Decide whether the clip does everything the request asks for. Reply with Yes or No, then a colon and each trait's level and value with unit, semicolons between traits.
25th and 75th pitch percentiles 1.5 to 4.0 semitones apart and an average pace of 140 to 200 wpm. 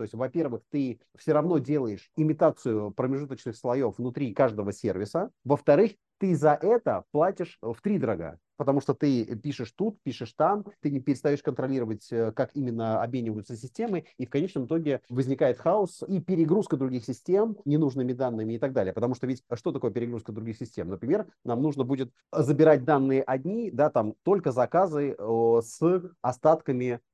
No: average, 4.4 semitones; fast, 160 wpm